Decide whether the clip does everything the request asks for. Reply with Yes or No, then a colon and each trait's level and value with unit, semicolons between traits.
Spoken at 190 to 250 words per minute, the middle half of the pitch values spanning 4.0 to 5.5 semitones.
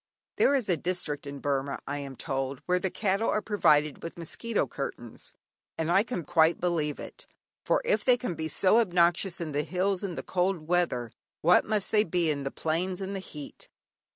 Yes: average, 200 wpm; average, 4.4 semitones